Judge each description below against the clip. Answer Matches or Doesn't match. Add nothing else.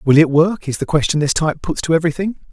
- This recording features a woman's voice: Doesn't match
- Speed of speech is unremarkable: Doesn't match